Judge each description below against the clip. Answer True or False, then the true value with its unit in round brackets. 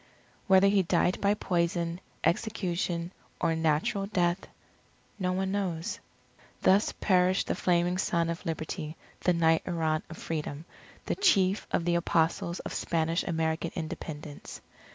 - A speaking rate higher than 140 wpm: False (135 wpm)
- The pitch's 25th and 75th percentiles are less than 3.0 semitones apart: True (2.4 semitones)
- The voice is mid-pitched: True (170 Hz)